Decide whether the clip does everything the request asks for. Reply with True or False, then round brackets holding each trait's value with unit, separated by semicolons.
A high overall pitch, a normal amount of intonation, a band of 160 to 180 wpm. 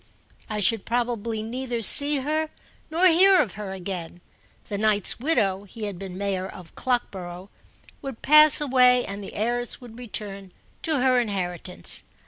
False (225 Hz; 4.7 semitones; 150 wpm)